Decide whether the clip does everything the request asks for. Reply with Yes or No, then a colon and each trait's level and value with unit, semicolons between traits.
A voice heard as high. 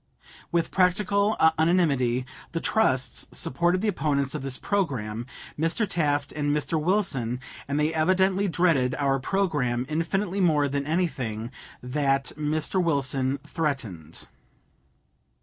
No: medium, 150 Hz